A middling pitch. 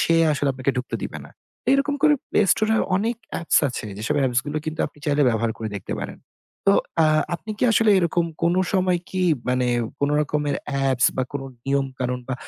Yes: medium, 145 Hz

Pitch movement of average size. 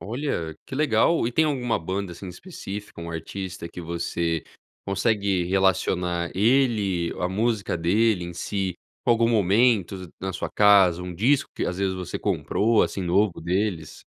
Yes: average, 4.1 semitones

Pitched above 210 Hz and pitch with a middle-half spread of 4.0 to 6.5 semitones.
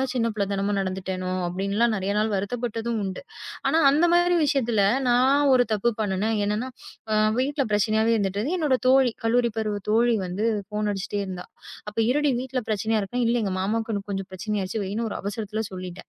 No: high, 220 Hz; average, 3.6 semitones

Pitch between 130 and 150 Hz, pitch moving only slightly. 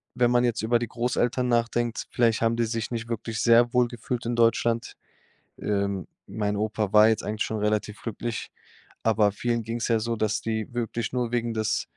No: low, 115 Hz; narrow, 1.6 semitones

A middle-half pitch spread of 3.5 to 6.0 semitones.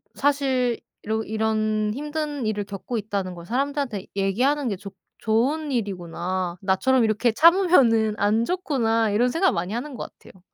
Yes: average, 5.2 semitones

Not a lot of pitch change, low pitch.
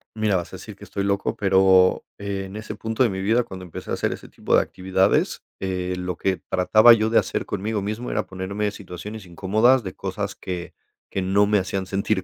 Yes: narrow, 2.3 semitones; low, 100 Hz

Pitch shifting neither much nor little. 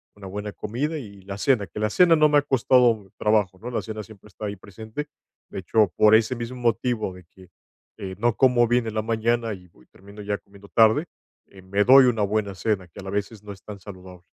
Yes: average, 3.1 semitones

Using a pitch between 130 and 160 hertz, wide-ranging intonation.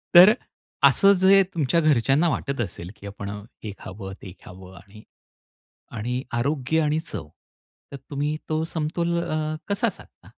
Yes: medium, 140 Hz; wide, 7.3 semitones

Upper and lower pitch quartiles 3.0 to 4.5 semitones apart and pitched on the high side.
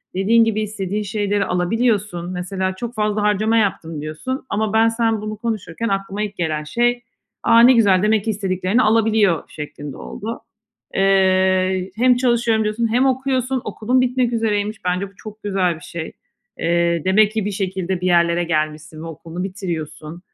Yes: average, 3.7 semitones; high, 205 Hz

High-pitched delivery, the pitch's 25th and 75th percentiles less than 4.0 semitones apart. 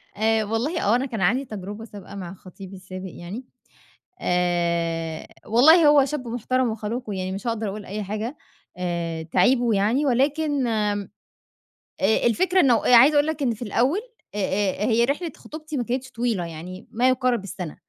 No: high, 225 Hz; average, 5.1 semitones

